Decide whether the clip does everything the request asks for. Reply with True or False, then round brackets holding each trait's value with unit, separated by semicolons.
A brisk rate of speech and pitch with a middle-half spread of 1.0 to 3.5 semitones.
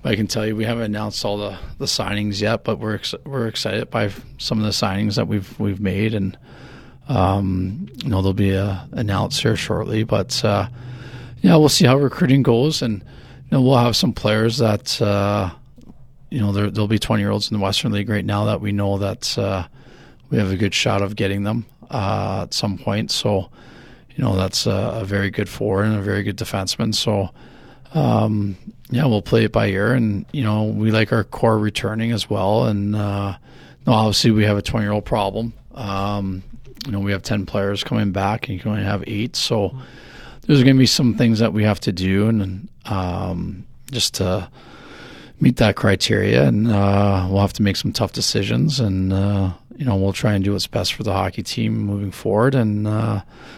True (210 wpm; 2.5 semitones)